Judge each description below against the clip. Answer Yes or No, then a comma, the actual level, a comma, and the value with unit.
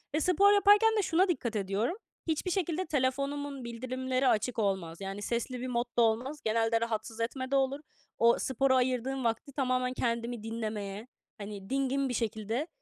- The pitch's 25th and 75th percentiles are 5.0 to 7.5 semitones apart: No, average, 3.5 semitones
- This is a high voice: Yes, very high, 250 Hz